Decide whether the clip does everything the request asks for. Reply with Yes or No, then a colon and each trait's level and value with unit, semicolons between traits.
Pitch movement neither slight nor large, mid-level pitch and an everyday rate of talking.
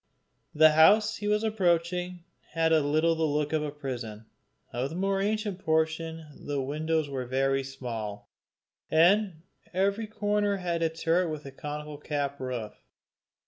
Yes: average, 4.2 semitones; medium, 160 Hz; average, 150 wpm